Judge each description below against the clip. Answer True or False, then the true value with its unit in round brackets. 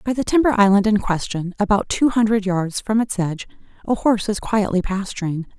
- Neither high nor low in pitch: False (205 Hz)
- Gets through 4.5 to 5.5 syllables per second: False (5.7 syllables/s)